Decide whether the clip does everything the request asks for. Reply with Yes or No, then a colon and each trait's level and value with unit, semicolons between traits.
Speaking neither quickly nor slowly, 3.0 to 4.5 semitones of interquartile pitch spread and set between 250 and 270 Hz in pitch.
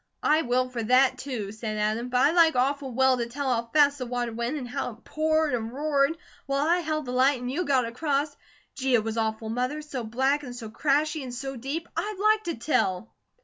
No: fast, 230 wpm; average, 3.7 semitones; very high, 260 Hz